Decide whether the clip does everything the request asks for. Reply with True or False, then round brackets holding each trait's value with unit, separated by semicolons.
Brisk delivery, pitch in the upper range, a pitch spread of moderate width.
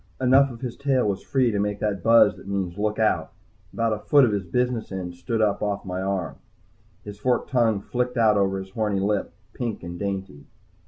False (210 wpm; 105 Hz; 3.5 semitones)